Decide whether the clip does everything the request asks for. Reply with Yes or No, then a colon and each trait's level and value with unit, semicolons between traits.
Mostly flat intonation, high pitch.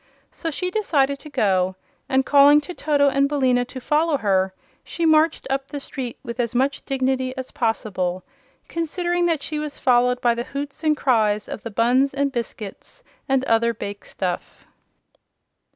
No: average, 3.9 semitones; very high, 265 Hz